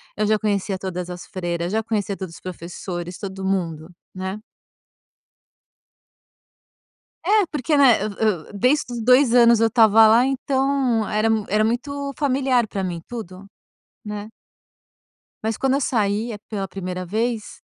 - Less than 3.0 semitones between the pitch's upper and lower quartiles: No, average, 4.5 semitones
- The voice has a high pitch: Yes, high, 215 Hz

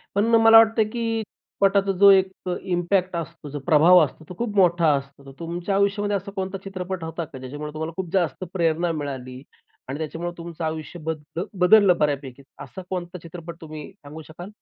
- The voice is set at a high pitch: No, medium, 175 Hz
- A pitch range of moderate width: Yes, average, 3.8 semitones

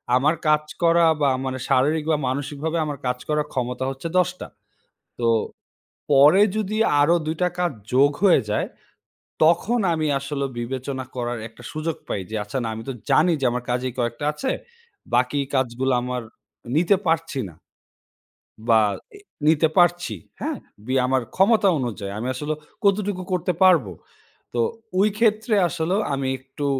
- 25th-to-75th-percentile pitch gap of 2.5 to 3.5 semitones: No, average, 5.1 semitones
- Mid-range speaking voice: Yes, medium, 145 Hz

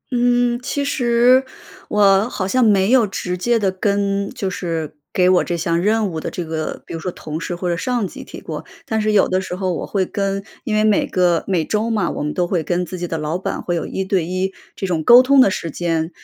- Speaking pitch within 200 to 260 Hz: No, high, 190 Hz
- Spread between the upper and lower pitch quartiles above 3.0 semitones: Yes, average, 3.7 semitones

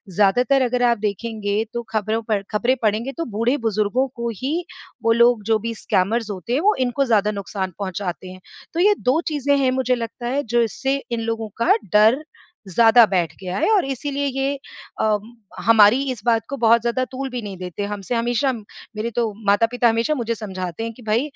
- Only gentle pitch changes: No, average, 3.2 semitones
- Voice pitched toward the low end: No, high, 230 Hz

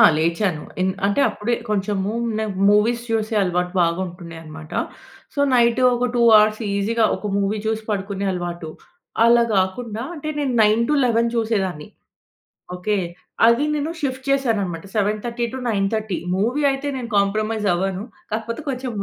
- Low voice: No, high, 215 Hz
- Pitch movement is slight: No, average, 3.5 semitones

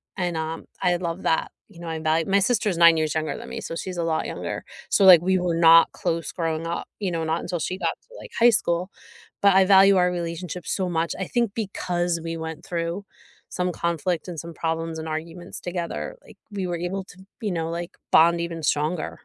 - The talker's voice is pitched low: No, medium, 170 Hz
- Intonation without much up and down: Yes, narrow, 2.0 semitones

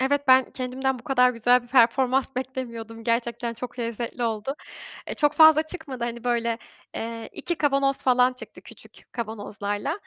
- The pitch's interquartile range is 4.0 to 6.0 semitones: No, narrow, 2.4 semitones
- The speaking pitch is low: No, very high, 250 Hz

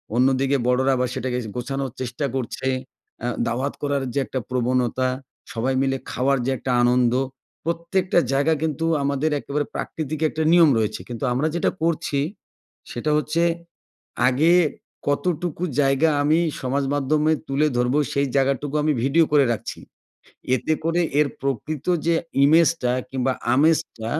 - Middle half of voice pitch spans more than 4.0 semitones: No, average, 3.2 semitones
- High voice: No, medium, 140 Hz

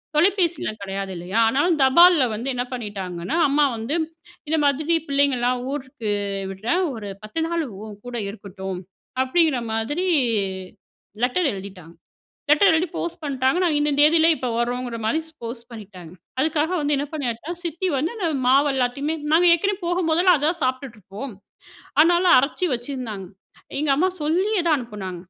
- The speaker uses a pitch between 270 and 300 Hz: Yes, very high, 275 Hz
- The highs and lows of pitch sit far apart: Yes, wide, 6.2 semitones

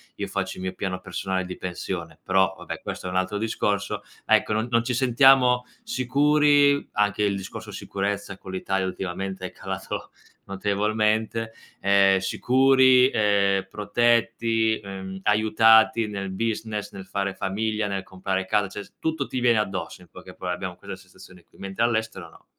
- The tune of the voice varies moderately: Yes, average, 3.1 semitones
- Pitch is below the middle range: Yes, low, 105 Hz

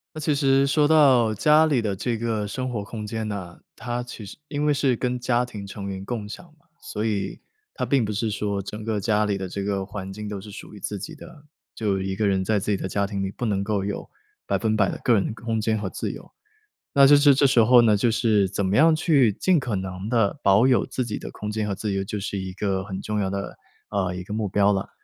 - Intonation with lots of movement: No, average, 3.7 semitones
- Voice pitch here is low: Yes, low, 105 Hz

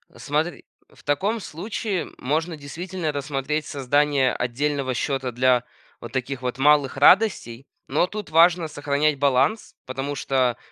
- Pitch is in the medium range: Yes, medium, 145 Hz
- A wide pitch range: No, average, 3.2 semitones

